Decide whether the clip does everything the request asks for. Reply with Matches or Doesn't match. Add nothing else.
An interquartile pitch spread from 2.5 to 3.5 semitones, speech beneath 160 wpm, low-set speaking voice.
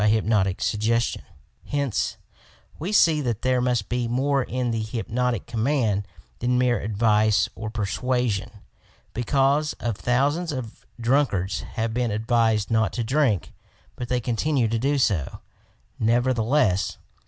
Matches